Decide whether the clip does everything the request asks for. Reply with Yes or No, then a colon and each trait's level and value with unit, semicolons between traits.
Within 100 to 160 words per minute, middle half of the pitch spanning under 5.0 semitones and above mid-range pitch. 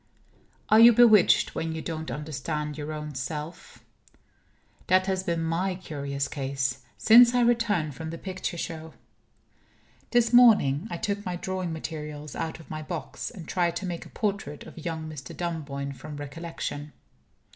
No: average, 155 wpm; average, 3.8 semitones; medium, 165 Hz